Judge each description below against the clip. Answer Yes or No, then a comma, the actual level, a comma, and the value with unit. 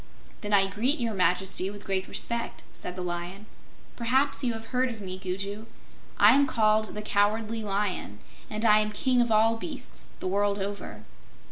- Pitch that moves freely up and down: No, average, 2.8 semitones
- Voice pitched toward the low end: No, high, 210 Hz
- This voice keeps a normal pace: Yes, average, 175 wpm